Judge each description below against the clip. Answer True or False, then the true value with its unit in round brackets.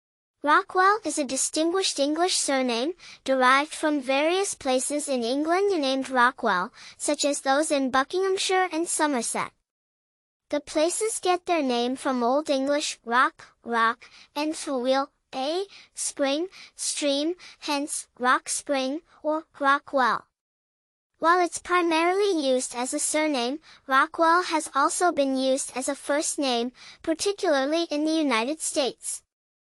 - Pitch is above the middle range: True (295 Hz)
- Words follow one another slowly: True (130 wpm)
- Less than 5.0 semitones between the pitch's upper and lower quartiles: True (3.7 semitones)